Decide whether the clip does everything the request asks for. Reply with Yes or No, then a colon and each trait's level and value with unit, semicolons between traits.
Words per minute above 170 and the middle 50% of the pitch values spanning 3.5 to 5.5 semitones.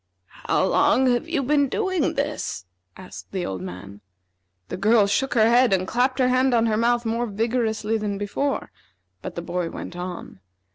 Yes: average, 180 wpm; average, 4.7 semitones